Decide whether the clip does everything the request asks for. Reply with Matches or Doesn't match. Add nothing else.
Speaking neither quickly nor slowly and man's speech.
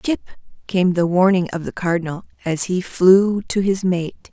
Doesn't match